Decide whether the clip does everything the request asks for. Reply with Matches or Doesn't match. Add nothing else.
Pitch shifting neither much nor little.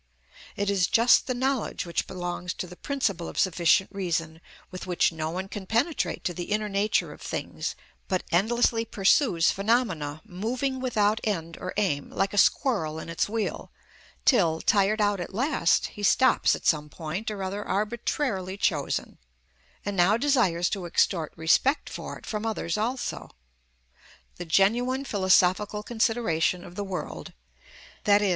Matches